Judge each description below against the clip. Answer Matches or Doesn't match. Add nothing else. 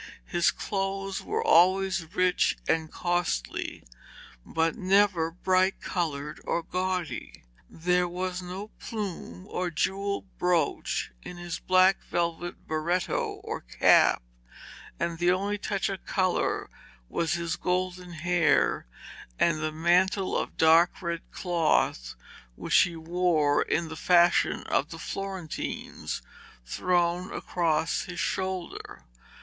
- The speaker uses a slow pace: Matches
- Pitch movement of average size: Doesn't match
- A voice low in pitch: Doesn't match